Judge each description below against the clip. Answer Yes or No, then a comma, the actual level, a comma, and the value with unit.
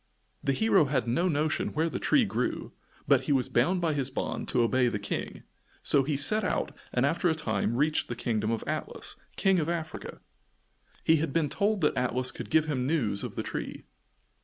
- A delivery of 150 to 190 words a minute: No, fast, 205 wpm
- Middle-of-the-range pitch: Yes, medium, 145 Hz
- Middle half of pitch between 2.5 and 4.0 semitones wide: No, average, 4.5 semitones